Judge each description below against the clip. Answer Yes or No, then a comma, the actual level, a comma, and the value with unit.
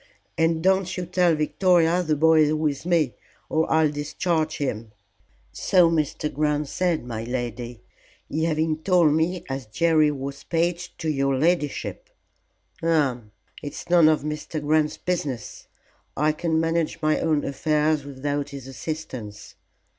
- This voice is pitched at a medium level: Yes, medium, 155 Hz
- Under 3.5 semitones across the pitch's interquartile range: Yes, average, 2.8 semitones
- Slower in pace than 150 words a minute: Yes, average, 140 wpm